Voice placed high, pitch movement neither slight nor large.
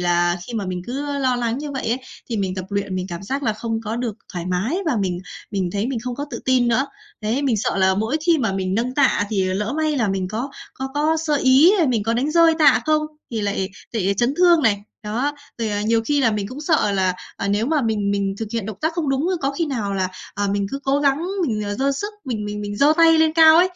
No: high, 230 Hz; wide, 5.8 semitones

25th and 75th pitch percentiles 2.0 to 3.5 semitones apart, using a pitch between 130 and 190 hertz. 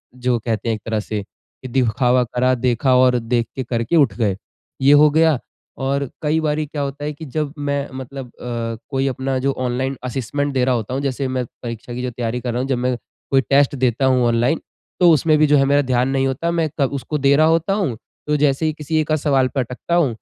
Yes: average, 2.8 semitones; low, 135 Hz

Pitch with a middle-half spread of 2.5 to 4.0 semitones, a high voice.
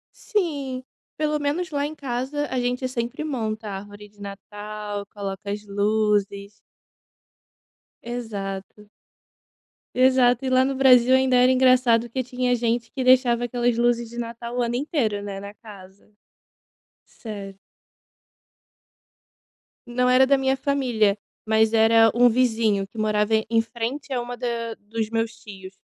Yes: average, 3.4 semitones; high, 235 Hz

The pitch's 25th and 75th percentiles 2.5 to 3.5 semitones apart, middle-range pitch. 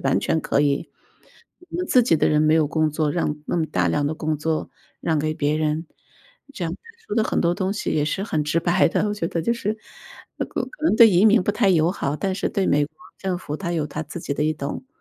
No: average, 4.2 semitones; medium, 160 Hz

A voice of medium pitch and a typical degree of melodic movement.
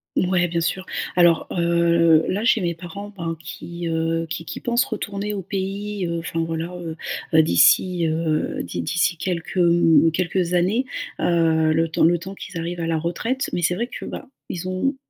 No: medium, 170 Hz; narrow, 2.3 semitones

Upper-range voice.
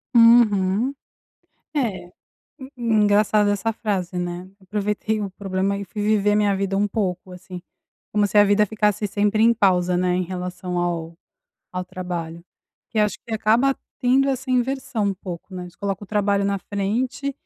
Yes: high, 205 Hz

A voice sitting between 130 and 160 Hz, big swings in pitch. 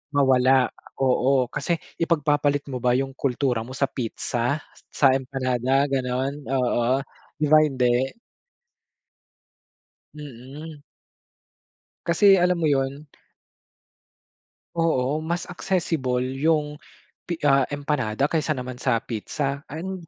No: low, 135 Hz; average, 3.0 semitones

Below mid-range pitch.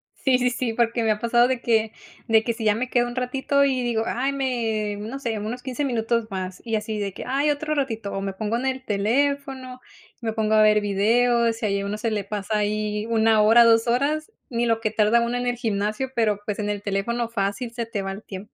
No: high, 225 Hz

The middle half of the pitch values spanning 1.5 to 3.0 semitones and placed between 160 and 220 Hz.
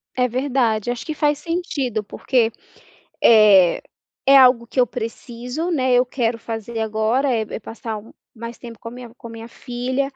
No: narrow, 2.5 semitones; high, 240 Hz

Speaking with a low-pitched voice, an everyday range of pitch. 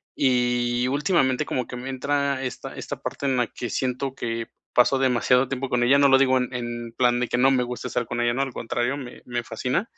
No: low, 125 Hz; narrow, 1.7 semitones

